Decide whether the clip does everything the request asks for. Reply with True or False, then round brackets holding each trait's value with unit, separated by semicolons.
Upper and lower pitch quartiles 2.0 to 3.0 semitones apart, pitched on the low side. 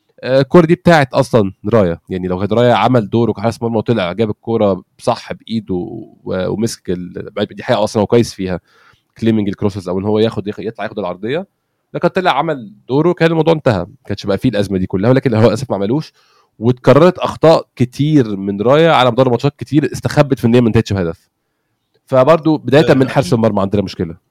False (4.9 semitones; 115 Hz)